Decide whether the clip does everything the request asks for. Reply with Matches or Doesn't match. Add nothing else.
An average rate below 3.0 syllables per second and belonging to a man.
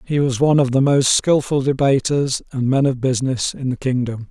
Doesn't match